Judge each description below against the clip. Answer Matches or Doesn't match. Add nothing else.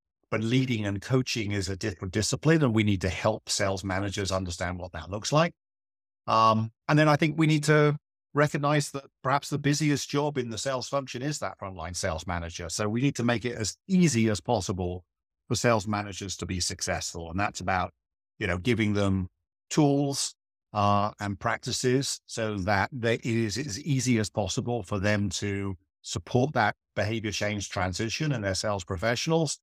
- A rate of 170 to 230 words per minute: Matches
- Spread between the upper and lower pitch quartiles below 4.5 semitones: Doesn't match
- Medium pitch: Doesn't match